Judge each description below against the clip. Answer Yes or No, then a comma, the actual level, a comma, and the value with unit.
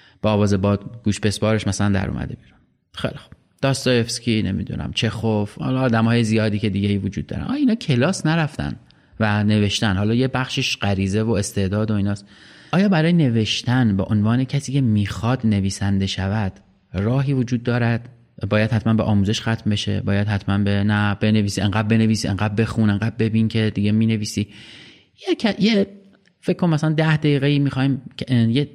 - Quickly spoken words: Yes, fast, 165 wpm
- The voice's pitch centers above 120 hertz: No, low, 110 Hz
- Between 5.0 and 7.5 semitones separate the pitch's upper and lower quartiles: No, average, 3.9 semitones